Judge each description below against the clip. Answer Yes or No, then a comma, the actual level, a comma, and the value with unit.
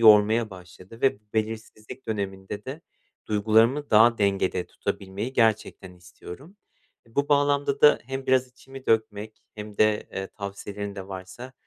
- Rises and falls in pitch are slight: No, average, 4.5 semitones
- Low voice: Yes, low, 110 Hz